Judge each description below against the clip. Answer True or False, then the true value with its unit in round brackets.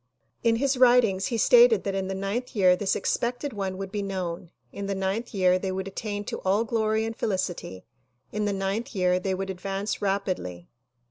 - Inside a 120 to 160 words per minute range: False (195 wpm)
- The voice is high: True (195 Hz)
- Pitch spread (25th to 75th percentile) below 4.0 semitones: True (2.8 semitones)